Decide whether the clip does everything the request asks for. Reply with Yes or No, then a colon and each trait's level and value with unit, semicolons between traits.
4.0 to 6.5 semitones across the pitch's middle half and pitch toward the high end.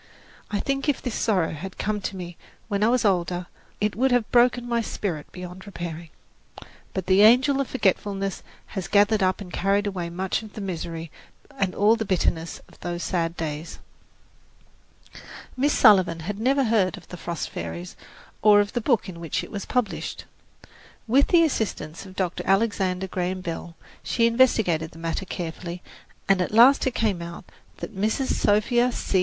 Yes: average, 4.3 semitones; high, 195 Hz